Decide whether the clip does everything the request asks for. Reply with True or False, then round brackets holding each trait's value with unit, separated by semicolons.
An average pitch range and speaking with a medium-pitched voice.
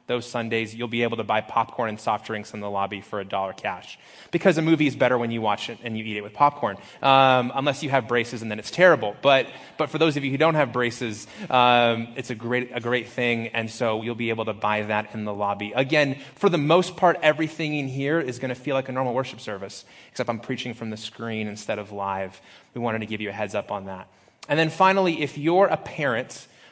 False (4.6 semitones; 120 Hz)